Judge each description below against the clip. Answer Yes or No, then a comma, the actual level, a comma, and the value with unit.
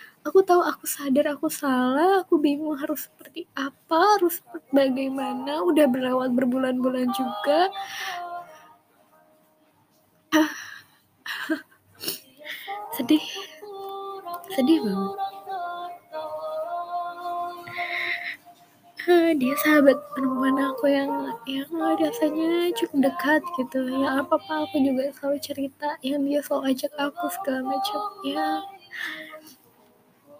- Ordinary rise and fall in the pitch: Yes, average, 4.4 semitones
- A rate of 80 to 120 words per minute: Yes, average, 95 wpm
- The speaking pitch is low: No, very high, 305 Hz